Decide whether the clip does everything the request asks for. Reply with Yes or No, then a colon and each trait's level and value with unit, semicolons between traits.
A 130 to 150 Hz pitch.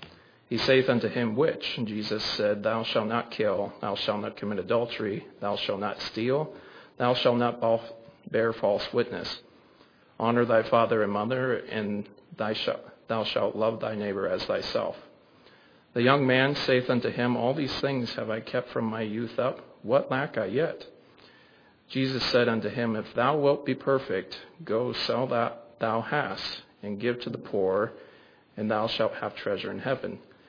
No: low, 120 Hz